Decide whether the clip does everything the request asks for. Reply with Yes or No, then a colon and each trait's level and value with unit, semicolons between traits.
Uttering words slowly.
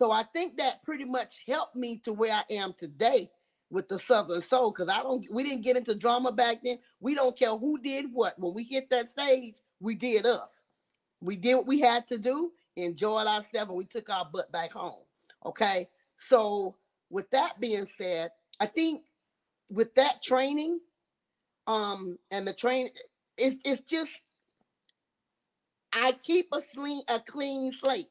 No: average, 175 wpm